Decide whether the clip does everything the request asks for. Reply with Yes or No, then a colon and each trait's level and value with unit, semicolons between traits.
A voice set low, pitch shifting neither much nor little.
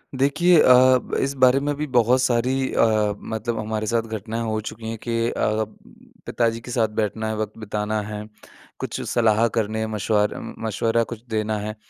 No: low, 115 Hz; narrow, 1.9 semitones